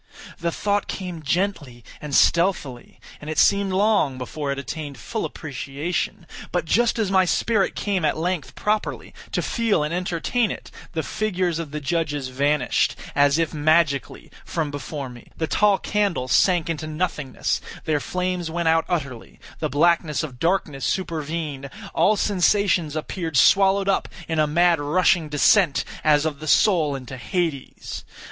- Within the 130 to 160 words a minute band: Yes, average, 155 wpm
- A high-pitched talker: No, medium, 160 Hz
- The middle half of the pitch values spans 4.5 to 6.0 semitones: No, average, 4.0 semitones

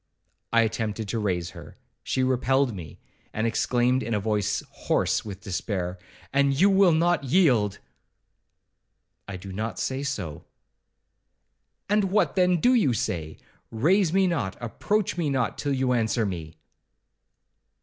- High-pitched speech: No, low, 120 Hz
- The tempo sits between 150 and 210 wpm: No, average, 140 wpm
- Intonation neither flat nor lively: No, wide, 7.4 semitones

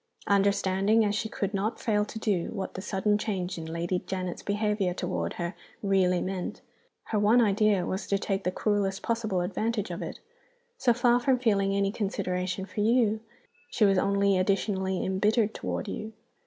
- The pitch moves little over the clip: Yes, narrow, 2.2 semitones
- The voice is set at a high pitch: Yes, high, 200 Hz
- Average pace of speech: Yes, average, 170 wpm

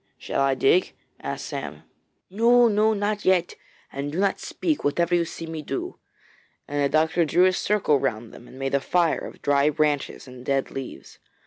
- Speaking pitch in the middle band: Yes, medium, 155 Hz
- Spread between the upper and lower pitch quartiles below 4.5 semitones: No, average, 5.2 semitones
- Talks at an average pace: Yes, average, 190 wpm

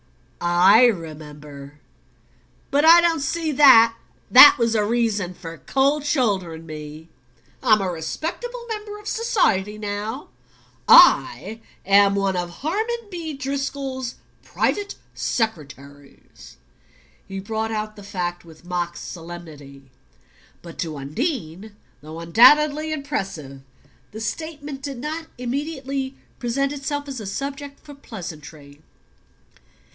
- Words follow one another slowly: Yes, slow, 110 wpm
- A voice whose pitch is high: Yes, high, 220 Hz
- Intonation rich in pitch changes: Yes, wide, 8.7 semitones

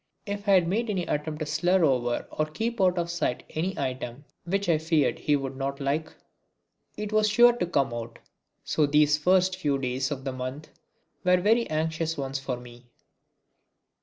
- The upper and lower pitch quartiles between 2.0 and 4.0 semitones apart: No, average, 5.2 semitones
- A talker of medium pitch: Yes, medium, 155 Hz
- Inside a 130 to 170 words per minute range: No, average, 180 wpm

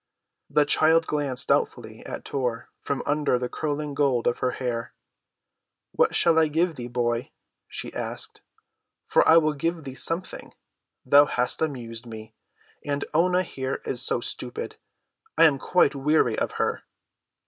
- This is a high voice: No, medium, 145 Hz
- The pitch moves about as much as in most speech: Yes, average, 4.3 semitones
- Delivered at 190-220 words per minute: No, average, 150 wpm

